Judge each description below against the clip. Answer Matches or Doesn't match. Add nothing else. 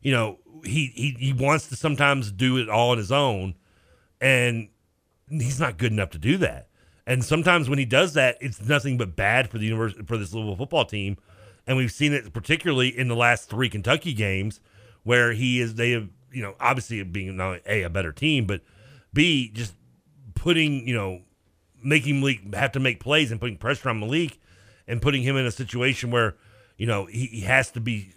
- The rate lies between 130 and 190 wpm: Doesn't match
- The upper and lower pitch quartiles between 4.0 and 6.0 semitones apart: Matches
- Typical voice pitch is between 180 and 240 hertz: Doesn't match